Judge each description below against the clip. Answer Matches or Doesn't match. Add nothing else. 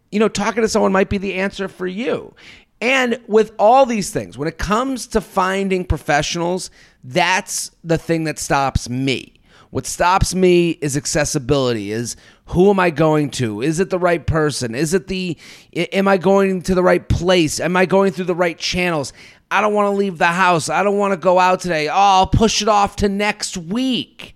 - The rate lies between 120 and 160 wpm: Doesn't match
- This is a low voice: Doesn't match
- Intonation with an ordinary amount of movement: Matches